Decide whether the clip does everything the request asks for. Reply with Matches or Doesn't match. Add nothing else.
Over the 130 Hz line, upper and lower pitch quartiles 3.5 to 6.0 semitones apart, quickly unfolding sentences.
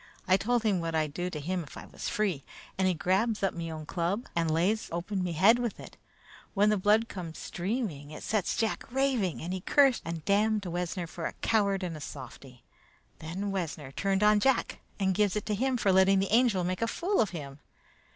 Matches